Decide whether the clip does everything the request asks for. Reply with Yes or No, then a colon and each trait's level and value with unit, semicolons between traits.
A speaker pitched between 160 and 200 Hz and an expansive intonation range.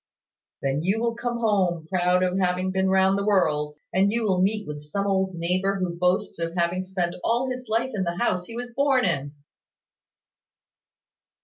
No: high, 190 Hz; average, 3.5 semitones